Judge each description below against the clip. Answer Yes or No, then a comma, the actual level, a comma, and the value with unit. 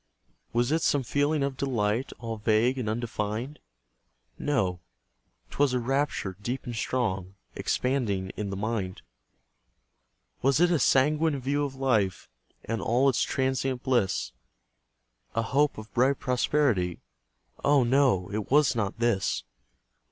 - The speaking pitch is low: Yes, low, 125 Hz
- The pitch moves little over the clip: No, average, 4.3 semitones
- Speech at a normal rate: No, slow, 130 wpm